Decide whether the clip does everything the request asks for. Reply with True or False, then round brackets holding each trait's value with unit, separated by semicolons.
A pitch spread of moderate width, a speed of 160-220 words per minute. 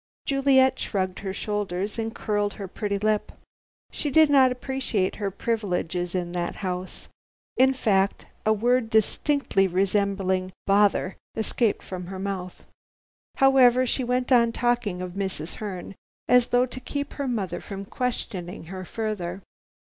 False (4.8 semitones; 140 wpm)